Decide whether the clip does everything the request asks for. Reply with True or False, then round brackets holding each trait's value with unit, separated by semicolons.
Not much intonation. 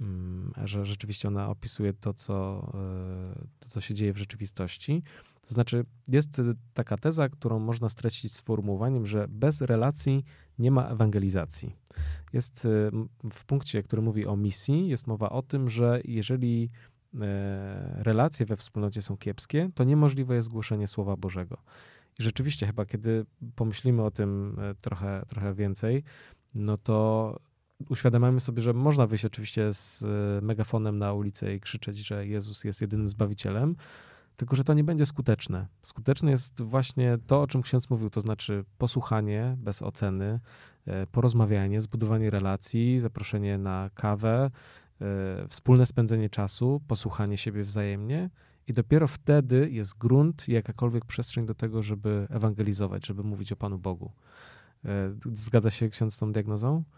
False (3.5 semitones)